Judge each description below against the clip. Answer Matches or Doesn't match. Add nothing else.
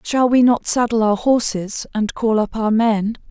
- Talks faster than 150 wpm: Matches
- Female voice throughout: Matches